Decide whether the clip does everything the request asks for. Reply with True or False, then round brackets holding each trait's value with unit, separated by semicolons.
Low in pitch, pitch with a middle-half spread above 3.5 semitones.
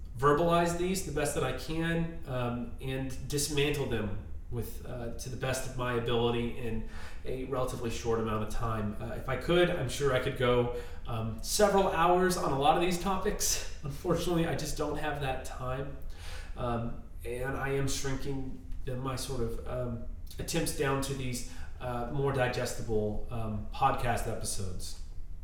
True (125 Hz; 3.9 semitones)